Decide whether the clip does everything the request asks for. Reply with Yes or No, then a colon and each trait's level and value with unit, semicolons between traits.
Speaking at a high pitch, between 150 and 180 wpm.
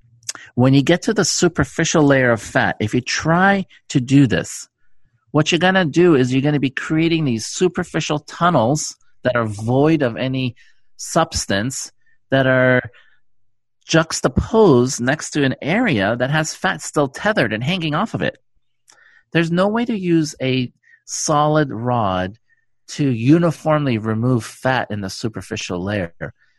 No: low, 135 Hz; average, 155 wpm